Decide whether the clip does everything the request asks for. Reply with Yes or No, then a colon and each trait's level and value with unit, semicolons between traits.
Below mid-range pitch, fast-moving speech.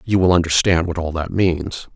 Yes: very low, 85 Hz; fast, 215 wpm